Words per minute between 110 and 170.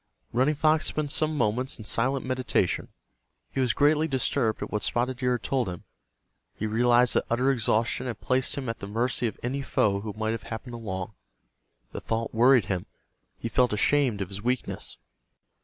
No: average, 185 wpm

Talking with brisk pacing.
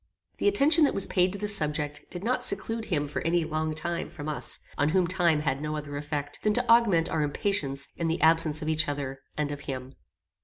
Yes: fast, 225 wpm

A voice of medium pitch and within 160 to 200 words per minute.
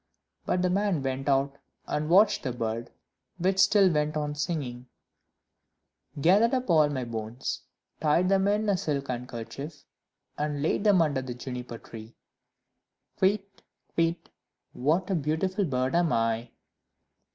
No: medium, 150 Hz; average, 140 wpm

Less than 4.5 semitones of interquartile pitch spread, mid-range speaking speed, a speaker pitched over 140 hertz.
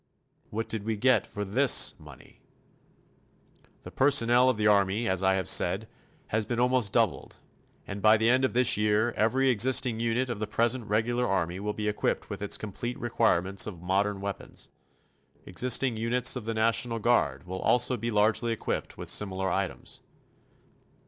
No: average, 3.2 semitones; average, 170 wpm; low, 110 Hz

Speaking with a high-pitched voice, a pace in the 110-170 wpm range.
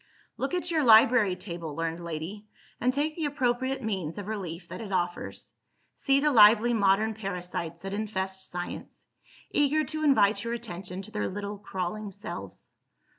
Yes: high, 210 Hz; average, 160 wpm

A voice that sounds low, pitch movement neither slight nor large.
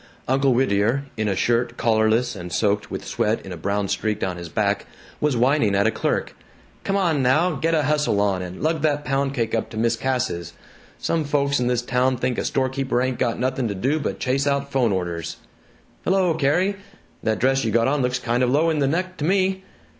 Yes: low, 130 Hz; average, 4.7 semitones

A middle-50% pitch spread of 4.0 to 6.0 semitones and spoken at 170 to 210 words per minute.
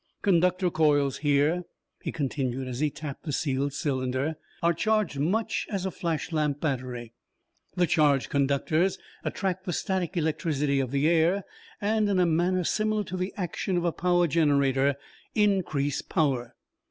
No: average, 4.5 semitones; average, 155 wpm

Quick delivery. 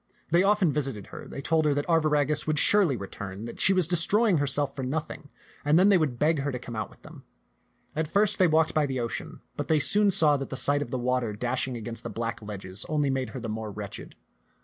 Yes: fast, 240 wpm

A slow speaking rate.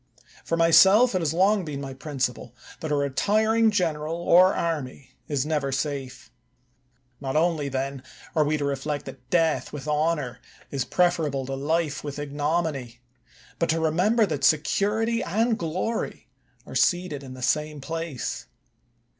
No: average, 145 wpm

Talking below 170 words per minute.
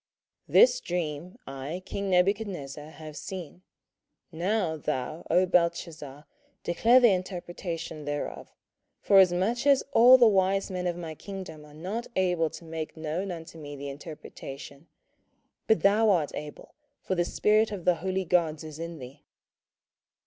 Yes: average, 145 wpm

